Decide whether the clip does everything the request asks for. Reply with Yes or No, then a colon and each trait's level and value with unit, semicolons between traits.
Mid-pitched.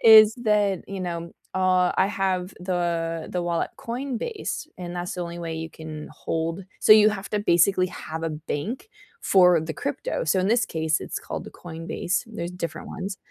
Yes: medium, 180 Hz